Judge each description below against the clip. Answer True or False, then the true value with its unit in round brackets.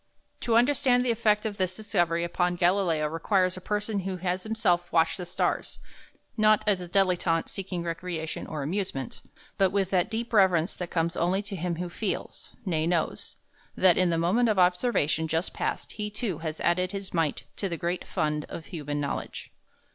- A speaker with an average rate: True (185 wpm)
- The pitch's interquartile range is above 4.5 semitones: False (3.2 semitones)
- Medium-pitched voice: True (180 Hz)